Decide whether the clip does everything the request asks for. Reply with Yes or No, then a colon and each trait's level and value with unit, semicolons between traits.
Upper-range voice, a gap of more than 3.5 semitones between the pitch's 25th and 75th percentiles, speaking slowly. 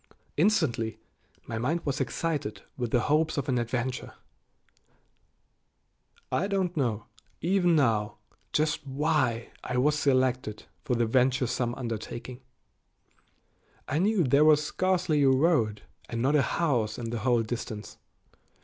No: low, 130 Hz; average, 4.7 semitones; slow, 130 wpm